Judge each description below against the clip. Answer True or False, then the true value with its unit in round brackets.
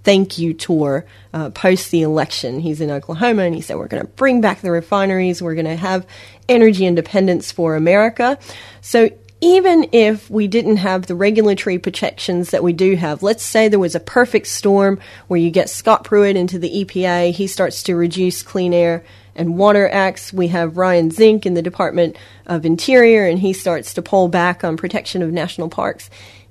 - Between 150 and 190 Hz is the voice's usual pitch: True (185 Hz)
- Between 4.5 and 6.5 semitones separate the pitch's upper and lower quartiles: False (3.3 semitones)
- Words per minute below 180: False (190 wpm)